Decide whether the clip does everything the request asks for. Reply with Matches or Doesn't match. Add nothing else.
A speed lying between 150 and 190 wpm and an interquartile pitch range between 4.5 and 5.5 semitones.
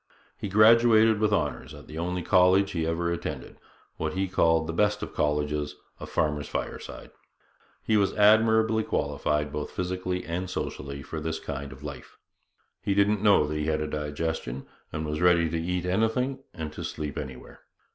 Matches